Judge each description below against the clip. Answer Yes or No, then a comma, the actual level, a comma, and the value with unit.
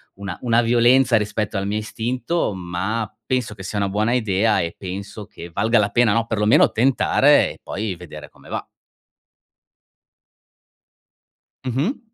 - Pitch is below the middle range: Yes, low, 110 Hz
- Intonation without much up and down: No, average, 3.3 semitones